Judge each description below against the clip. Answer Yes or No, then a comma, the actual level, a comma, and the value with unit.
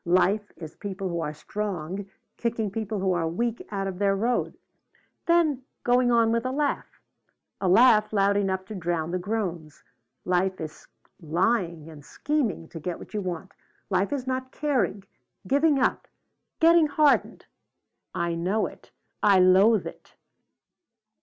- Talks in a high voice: Yes, high, 200 Hz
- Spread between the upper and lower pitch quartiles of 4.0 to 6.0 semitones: Yes, average, 4.8 semitones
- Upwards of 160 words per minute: No, average, 150 wpm